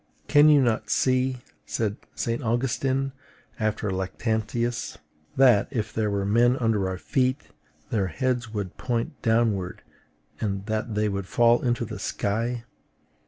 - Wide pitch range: No, average, 2.9 semitones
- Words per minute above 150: No, slow, 135 wpm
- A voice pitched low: Yes, low, 115 Hz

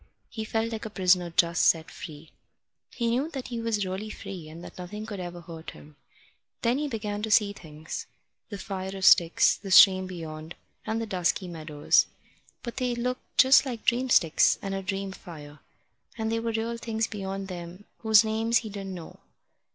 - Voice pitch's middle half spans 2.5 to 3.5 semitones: No, average, 4.4 semitones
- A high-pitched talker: Yes, high, 195 Hz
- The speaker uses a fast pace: No, average, 190 wpm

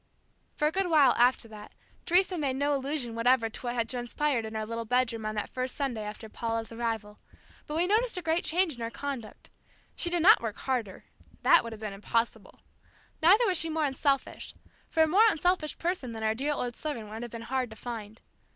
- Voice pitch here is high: Yes, very high, 250 Hz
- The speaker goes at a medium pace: No, fast, 215 wpm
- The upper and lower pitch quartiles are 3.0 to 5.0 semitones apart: No, wide, 5.5 semitones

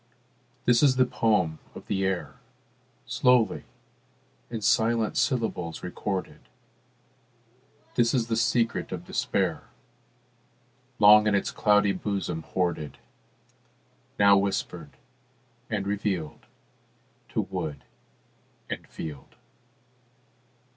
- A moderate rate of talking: No, slow, 90 wpm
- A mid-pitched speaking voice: No, low, 105 Hz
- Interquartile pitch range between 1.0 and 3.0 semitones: No, average, 3.8 semitones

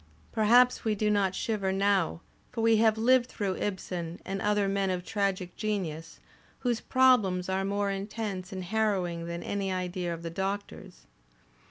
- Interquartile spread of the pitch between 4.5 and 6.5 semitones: No, average, 2.7 semitones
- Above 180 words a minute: No, average, 160 wpm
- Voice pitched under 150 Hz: No, high, 195 Hz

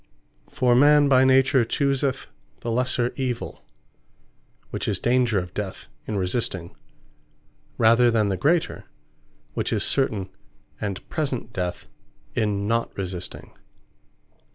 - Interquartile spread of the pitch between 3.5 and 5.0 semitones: Yes, average, 4.7 semitones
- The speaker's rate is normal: No, slow, 115 wpm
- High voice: No, low, 120 Hz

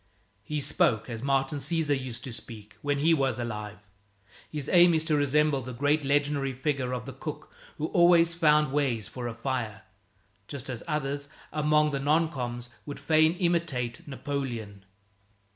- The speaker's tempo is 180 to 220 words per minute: No, average, 160 wpm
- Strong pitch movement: No, average, 3.6 semitones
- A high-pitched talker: No, medium, 140 Hz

